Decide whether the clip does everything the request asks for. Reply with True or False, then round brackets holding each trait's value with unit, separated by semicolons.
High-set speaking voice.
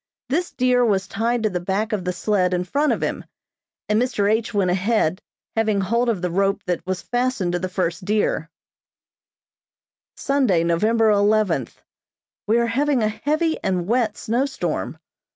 True (210 Hz)